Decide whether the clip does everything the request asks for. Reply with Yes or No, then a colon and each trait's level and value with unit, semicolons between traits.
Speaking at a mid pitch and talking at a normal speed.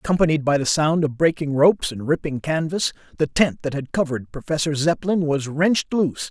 Yes: medium, 150 Hz; average, 190 wpm